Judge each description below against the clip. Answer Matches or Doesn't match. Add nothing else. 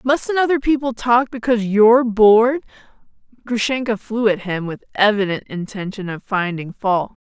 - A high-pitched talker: Matches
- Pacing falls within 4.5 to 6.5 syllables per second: Matches